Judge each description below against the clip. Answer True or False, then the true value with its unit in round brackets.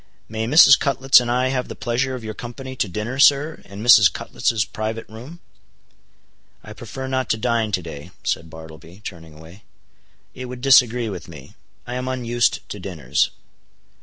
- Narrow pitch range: False (4.7 semitones)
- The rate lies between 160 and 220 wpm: True (170 wpm)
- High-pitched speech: False (115 Hz)